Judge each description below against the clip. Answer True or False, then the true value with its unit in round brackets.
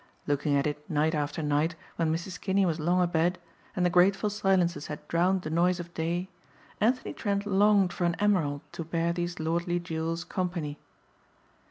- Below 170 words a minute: False (175 wpm)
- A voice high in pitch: False (175 Hz)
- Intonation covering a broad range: False (2.5 semitones)